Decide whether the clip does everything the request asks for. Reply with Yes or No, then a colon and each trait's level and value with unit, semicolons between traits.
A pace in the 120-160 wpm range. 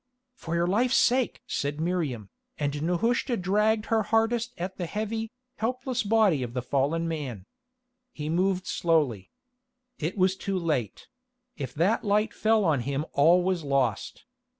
Yes: average, 150 wpm